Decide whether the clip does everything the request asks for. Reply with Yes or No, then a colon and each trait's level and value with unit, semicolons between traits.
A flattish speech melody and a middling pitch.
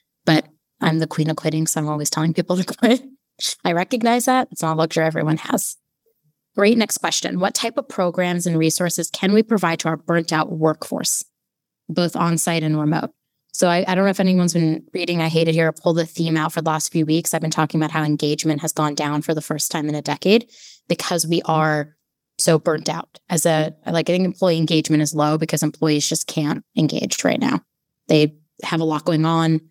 Yes: narrow, 2.1 semitones; medium, 160 Hz